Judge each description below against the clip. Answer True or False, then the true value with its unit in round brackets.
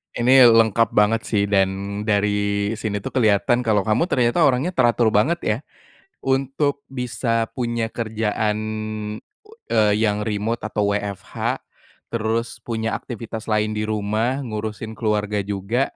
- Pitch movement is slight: True (2.3 semitones)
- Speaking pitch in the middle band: False (110 Hz)